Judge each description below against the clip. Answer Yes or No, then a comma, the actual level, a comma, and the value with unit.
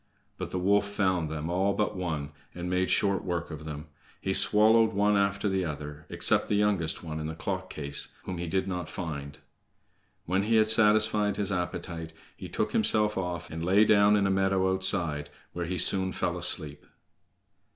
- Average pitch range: Yes, average, 3.8 semitones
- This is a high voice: No, very low, 95 Hz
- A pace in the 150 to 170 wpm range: No, average, 185 wpm